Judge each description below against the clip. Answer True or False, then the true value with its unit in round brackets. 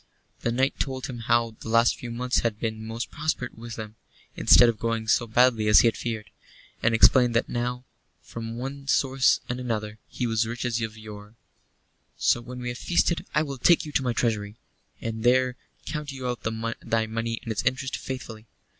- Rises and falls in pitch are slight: True (2.2 semitones)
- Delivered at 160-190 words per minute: False (200 wpm)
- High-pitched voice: False (120 Hz)